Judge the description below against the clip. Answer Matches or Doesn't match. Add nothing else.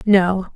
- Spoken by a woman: Matches